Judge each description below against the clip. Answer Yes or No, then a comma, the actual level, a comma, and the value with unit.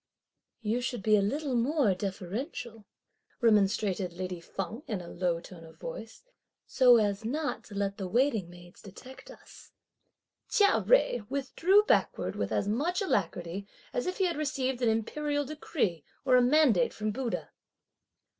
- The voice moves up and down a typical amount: No, wide, 6.3 semitones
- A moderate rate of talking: Yes, average, 155 wpm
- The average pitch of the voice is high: Yes, high, 225 Hz